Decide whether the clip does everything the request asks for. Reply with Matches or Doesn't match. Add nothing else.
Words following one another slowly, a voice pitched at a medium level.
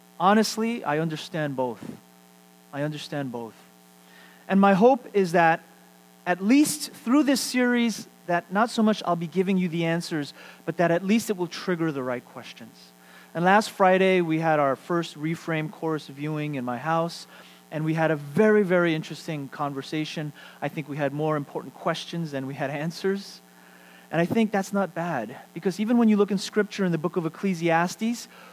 Doesn't match